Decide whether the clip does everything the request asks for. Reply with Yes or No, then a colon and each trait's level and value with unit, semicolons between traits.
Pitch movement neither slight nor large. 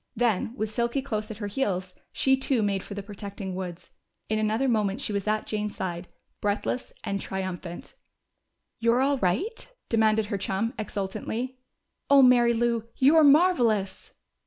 Yes: average, 3.6 semitones